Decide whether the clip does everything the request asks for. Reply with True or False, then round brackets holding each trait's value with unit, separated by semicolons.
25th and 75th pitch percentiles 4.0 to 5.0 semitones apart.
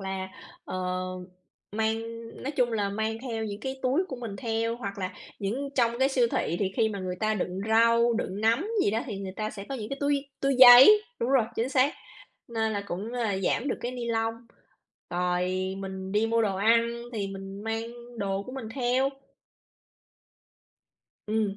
False (3.6 semitones)